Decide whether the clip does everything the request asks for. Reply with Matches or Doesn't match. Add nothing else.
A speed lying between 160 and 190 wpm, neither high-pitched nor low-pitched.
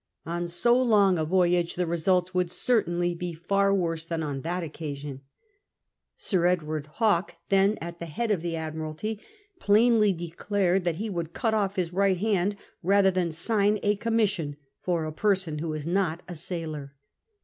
Matches